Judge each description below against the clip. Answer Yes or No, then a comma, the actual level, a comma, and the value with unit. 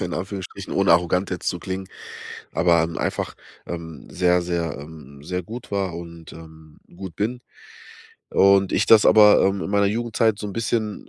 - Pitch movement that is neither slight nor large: Yes, average, 3.3 semitones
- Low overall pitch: Yes, very low, 95 Hz